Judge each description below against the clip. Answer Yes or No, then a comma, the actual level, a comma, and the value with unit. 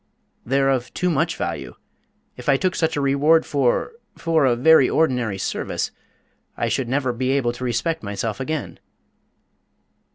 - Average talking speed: Yes, average, 155 wpm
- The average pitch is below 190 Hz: Yes, low, 135 Hz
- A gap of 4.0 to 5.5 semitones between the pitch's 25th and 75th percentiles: Yes, average, 4.5 semitones